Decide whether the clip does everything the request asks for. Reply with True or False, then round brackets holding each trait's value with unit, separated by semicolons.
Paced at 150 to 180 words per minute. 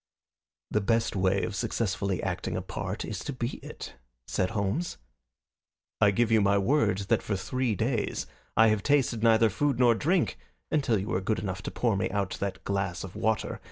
False (190 wpm)